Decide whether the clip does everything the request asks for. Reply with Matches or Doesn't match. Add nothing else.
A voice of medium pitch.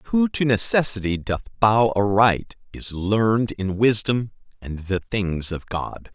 Doesn't match